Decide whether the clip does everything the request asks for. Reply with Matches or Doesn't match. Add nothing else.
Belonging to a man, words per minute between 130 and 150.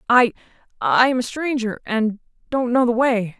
Doesn't match